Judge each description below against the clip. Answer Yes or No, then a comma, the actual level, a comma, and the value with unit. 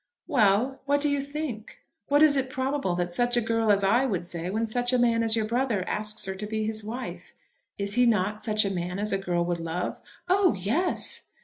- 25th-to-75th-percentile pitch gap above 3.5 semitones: Yes, average, 4.9 semitones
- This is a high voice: Yes, high, 220 Hz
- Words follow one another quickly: Yes, fast, 225 wpm